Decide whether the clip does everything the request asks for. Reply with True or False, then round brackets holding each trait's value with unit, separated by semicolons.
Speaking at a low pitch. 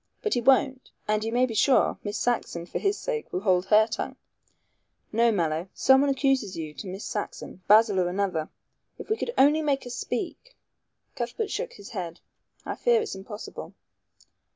False (225 Hz)